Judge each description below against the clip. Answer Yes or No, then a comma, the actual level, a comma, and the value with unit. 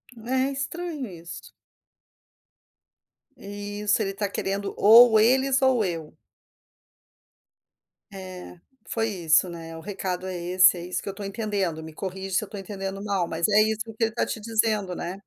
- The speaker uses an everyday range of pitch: Yes, average, 3.3 semitones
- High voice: Yes, high, 200 Hz